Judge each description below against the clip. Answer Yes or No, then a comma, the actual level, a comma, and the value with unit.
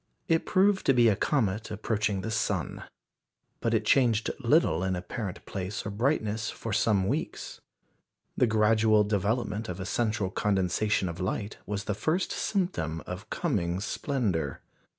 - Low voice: Yes, low, 105 Hz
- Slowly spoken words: No, average, 150 wpm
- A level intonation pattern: No, average, 3.3 semitones